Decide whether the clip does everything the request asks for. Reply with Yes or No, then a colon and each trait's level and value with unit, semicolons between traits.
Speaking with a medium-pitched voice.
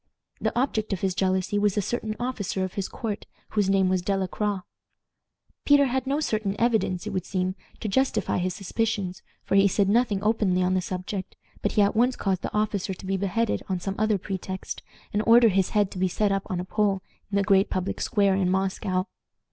No: high, 195 Hz